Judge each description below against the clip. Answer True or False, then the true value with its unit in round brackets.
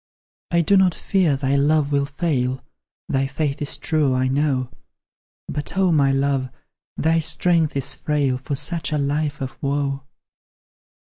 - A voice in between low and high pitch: True (145 Hz)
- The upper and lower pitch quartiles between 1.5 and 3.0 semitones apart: True (2.4 semitones)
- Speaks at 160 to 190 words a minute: False (150 wpm)